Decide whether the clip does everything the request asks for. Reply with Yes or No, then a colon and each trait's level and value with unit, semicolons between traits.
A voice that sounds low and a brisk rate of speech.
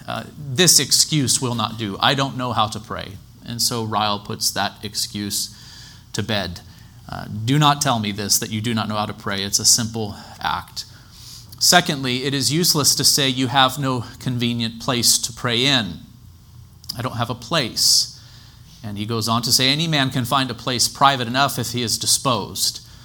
No: low, 120 Hz; average, 195 wpm